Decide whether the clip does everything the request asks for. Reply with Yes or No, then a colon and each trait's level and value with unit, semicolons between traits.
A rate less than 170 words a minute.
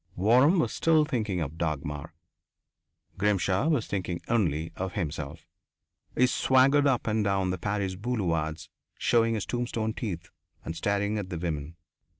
Yes: average, 145 wpm